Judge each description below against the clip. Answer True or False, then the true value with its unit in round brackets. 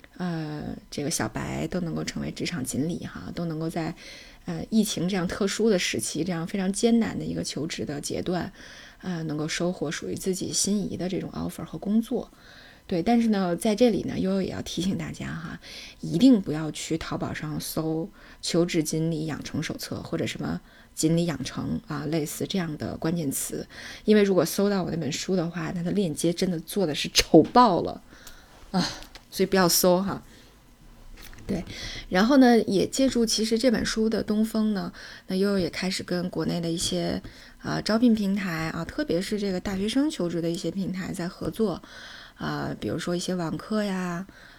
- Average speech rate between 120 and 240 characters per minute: False (280 characters per minute)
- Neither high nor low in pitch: True (180 Hz)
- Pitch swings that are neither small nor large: True (4.3 semitones)